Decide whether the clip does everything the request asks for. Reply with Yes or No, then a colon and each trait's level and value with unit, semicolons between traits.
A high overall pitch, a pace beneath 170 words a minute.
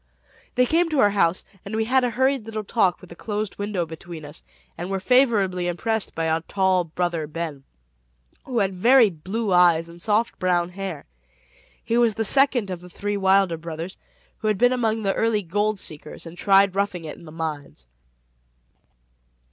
No: high, 195 Hz; average, 185 wpm